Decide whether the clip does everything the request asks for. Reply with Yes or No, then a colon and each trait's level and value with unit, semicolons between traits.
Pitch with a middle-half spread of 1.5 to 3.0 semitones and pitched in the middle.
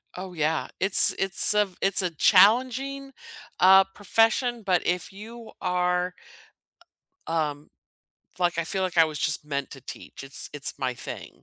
No: average, 4.4 semitones; medium, 180 Hz